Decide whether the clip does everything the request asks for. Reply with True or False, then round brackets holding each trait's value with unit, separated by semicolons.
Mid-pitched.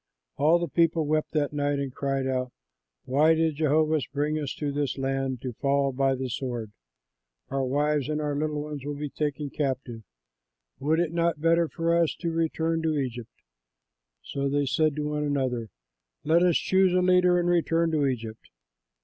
True (150 Hz)